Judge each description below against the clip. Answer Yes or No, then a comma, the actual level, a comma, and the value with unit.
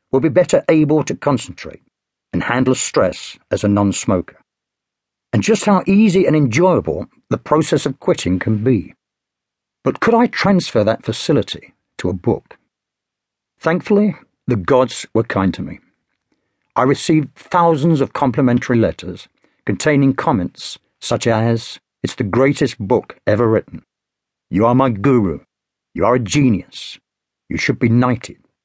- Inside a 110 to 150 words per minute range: Yes, average, 140 wpm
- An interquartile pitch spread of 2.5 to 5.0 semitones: No, wide, 5.5 semitones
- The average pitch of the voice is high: No, low, 135 Hz